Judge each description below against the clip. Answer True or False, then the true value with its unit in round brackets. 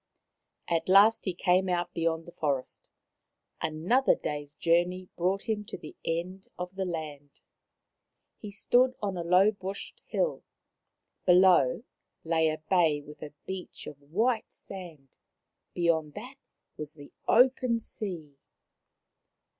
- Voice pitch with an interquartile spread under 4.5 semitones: True (3.8 semitones)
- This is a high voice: False (175 Hz)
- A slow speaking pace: True (130 wpm)